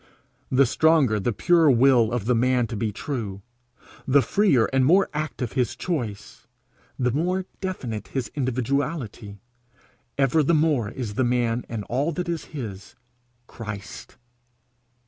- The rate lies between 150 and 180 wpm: No, average, 140 wpm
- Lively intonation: No, average, 4.8 semitones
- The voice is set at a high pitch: No, low, 125 Hz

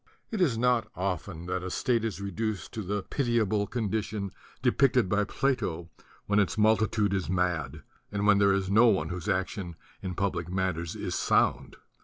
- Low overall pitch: Yes, low, 100 Hz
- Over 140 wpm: Yes, average, 170 wpm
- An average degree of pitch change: Yes, average, 3.1 semitones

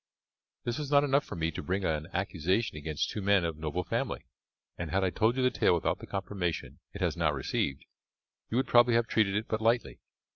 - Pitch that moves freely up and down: Yes, wide, 5.8 semitones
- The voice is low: Yes, very low, 95 Hz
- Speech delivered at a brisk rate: Yes, fast, 220 wpm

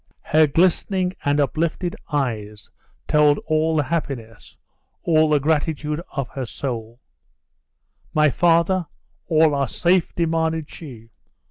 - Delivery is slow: Yes, slow, 115 wpm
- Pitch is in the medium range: Yes, medium, 150 Hz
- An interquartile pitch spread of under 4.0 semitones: Yes, average, 3.0 semitones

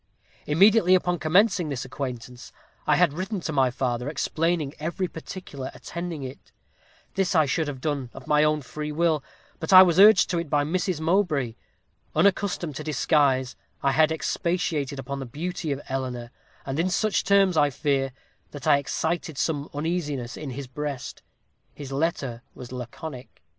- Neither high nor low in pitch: Yes, medium, 150 Hz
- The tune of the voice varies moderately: Yes, average, 4.3 semitones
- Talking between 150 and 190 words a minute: Yes, average, 165 wpm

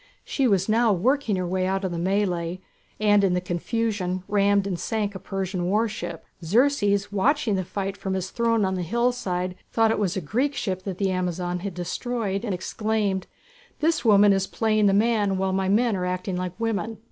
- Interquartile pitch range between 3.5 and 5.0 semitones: No, average, 3.1 semitones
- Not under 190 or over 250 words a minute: Yes, average, 195 wpm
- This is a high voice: Yes, high, 195 Hz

